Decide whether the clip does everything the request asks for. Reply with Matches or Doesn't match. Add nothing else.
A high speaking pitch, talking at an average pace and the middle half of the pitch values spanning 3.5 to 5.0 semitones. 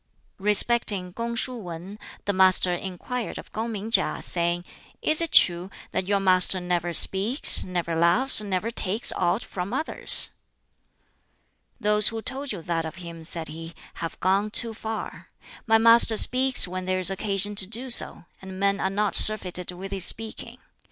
Matches